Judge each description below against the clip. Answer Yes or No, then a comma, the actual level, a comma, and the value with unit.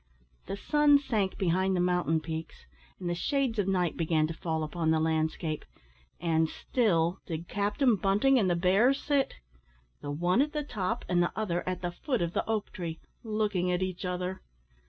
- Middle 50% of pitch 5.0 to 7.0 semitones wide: No, average, 4.5 semitones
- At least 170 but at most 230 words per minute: Yes, average, 185 wpm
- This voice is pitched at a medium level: Yes, medium, 180 Hz